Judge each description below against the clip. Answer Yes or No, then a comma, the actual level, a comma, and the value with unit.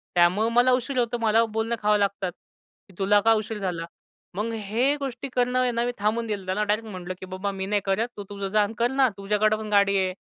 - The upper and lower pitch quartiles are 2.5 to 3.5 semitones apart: Yes, average, 2.9 semitones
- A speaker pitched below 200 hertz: No, high, 210 Hz